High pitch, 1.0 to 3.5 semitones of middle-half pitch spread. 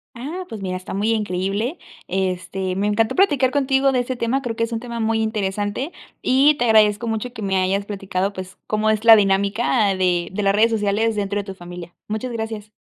Yes: high, 215 Hz; average, 3.2 semitones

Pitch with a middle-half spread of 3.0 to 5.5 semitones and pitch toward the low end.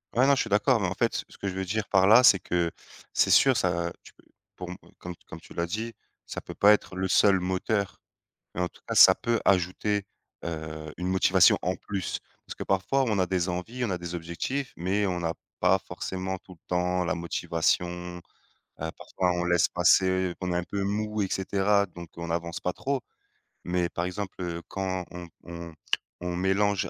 No: narrow, 2.4 semitones; very low, 90 Hz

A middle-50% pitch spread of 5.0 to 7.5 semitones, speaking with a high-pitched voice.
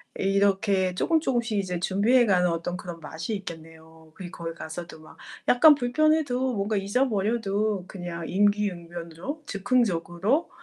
Yes: wide, 5.5 semitones; high, 195 Hz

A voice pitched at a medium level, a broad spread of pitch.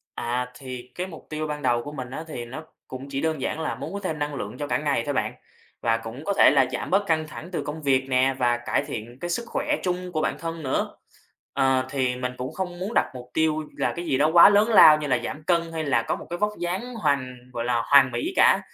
No: medium, 145 Hz; average, 4.8 semitones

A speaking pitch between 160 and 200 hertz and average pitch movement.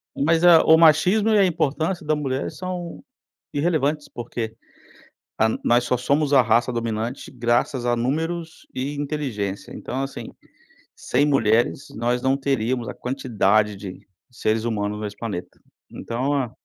No: low, 130 Hz; average, 4.4 semitones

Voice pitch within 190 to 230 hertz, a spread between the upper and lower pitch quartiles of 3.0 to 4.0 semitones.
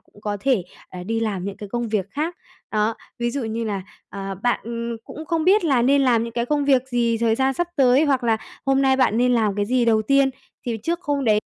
No: high, 240 Hz; average, 3.7 semitones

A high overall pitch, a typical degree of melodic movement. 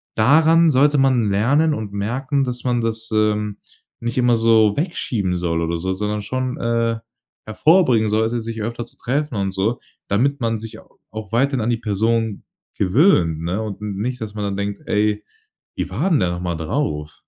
No: low, 110 Hz; average, 3.8 semitones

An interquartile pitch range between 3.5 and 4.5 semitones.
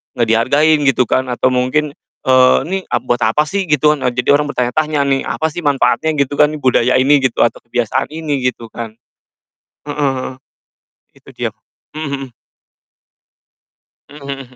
No: average, 3.0 semitones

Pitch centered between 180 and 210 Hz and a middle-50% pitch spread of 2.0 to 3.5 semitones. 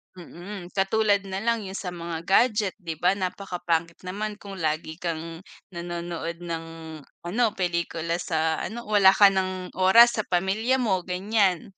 Yes: medium, 185 Hz; average, 2.9 semitones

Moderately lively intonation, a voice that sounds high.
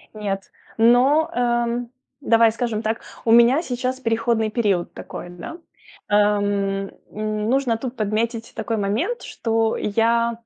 No: narrow, 2.3 semitones; high, 225 Hz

